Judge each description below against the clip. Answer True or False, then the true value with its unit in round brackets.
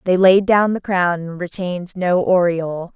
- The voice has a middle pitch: True (180 Hz)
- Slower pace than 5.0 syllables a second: True (4.6 syllables/s)